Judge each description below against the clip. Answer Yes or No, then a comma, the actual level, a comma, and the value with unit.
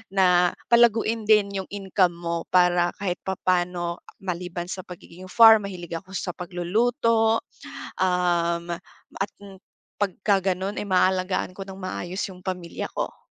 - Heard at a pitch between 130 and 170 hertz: No, medium, 185 Hz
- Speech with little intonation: Yes, narrow, 2.1 semitones